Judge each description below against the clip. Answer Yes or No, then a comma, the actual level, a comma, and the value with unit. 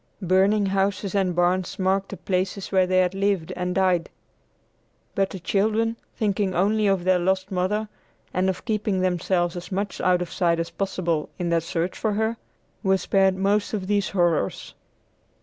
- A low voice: No, high, 190 Hz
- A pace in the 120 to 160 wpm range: No, average, 170 wpm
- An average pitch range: No, narrow, 1.8 semitones